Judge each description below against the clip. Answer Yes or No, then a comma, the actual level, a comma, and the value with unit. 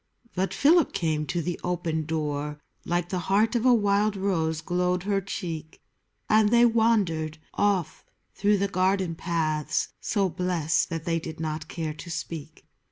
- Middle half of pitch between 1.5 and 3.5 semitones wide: No, average, 3.9 semitones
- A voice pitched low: No, medium, 175 Hz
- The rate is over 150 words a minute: Yes, average, 160 wpm